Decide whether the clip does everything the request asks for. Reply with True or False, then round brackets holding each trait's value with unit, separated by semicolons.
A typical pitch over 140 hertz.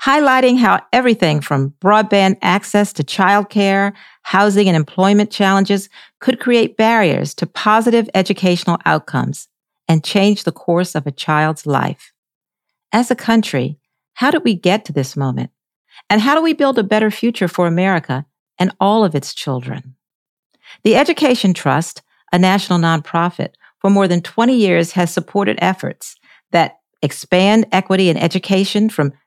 True (190 Hz)